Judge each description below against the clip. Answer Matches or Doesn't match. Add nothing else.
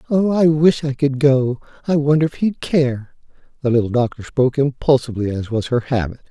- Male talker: Matches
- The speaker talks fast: Doesn't match